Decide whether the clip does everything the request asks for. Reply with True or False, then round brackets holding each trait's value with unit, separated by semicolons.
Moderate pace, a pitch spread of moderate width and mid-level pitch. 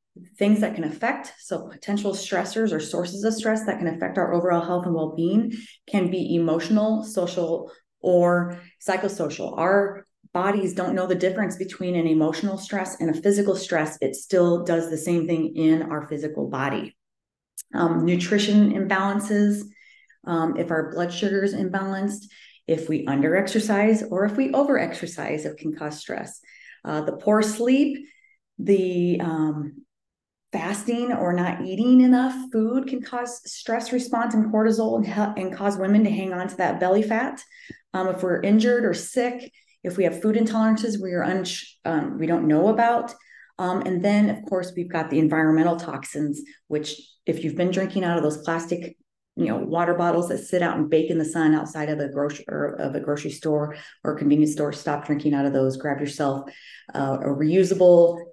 True (180 wpm; 4.6 semitones; 180 Hz)